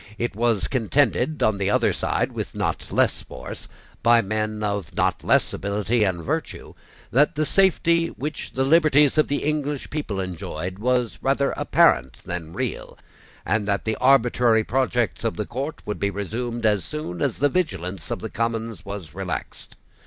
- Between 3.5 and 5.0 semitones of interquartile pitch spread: No, wide, 5.4 semitones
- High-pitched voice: No, low, 115 Hz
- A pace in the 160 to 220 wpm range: Yes, average, 165 wpm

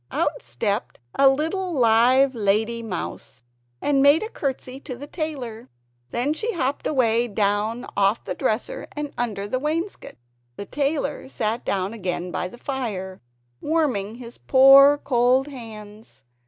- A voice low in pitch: No, high, 245 Hz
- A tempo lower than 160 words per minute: Yes, average, 140 wpm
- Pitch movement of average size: Yes, average, 4.8 semitones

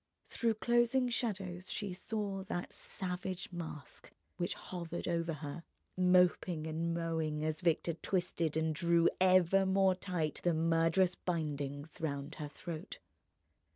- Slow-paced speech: Yes, slow, 125 wpm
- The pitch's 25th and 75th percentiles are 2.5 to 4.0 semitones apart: Yes, average, 2.8 semitones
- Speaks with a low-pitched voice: No, medium, 175 Hz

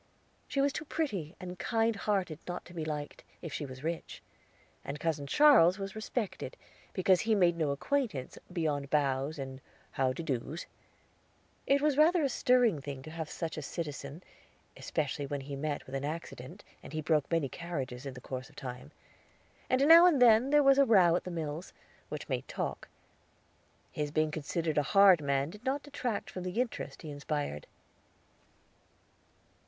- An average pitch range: No, wide, 7.1 semitones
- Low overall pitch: No, medium, 165 Hz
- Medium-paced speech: Yes, average, 175 wpm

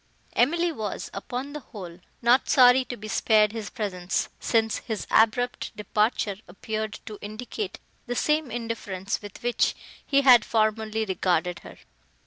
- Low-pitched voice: No, high, 220 Hz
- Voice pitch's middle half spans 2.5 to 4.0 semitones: Yes, average, 3.0 semitones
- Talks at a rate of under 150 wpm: Yes, average, 140 wpm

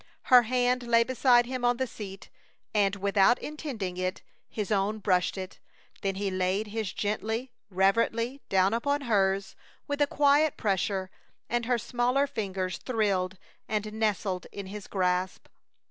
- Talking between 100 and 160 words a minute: Yes, average, 145 wpm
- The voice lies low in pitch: No, high, 210 Hz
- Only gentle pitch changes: No, average, 4.0 semitones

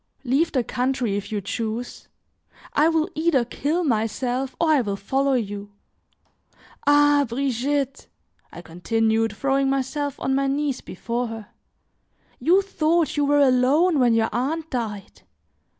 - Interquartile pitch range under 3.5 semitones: No, average, 4.3 semitones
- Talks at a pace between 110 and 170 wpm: Yes, slow, 135 wpm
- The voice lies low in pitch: No, very high, 265 Hz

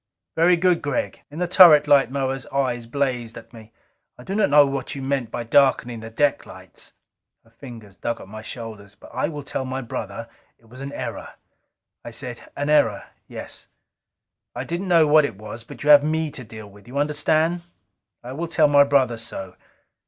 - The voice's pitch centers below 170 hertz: Yes, low, 135 Hz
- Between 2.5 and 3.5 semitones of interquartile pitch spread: No, average, 4.4 semitones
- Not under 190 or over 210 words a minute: Yes, average, 195 wpm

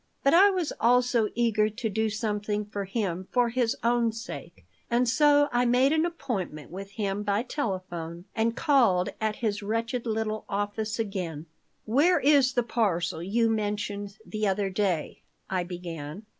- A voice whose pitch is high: Yes, high, 215 Hz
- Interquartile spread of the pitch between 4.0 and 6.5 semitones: No, average, 3.5 semitones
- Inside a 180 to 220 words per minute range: No, average, 155 wpm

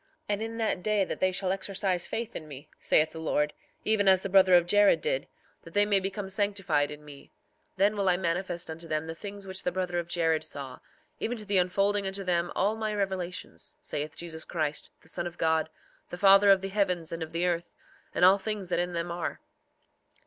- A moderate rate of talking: No, fast, 220 wpm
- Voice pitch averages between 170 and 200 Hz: Yes, medium, 185 Hz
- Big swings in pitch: No, average, 3.1 semitones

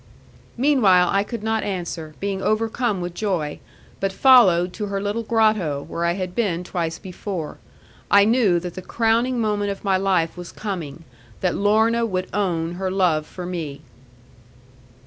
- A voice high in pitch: Yes, high, 195 Hz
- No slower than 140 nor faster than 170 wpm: Yes, average, 160 wpm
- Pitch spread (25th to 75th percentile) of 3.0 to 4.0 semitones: Yes, average, 3.6 semitones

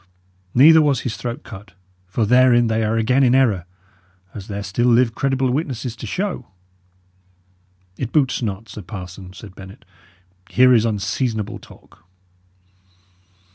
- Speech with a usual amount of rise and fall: Yes, average, 3.8 semitones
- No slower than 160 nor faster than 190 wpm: No, slow, 135 wpm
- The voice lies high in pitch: No, low, 115 Hz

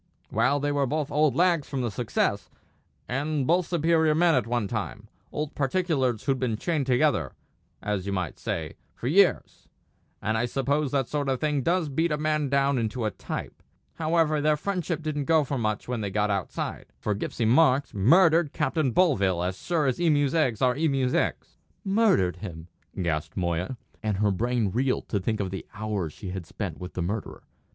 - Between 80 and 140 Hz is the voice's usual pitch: Yes, low, 135 Hz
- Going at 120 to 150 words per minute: No, average, 190 wpm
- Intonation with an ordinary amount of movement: No, wide, 6.4 semitones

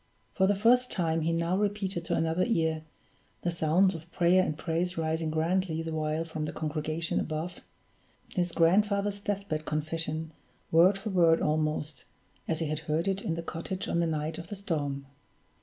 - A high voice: No, medium, 165 Hz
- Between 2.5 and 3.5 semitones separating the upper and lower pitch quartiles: Yes, average, 3.0 semitones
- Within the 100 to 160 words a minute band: No, average, 180 wpm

